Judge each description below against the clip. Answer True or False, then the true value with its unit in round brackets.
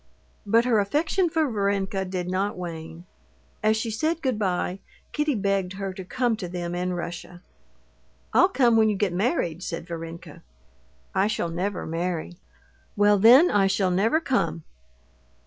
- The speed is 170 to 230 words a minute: False (155 wpm)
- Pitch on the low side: False (195 Hz)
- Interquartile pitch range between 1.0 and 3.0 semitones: False (4.1 semitones)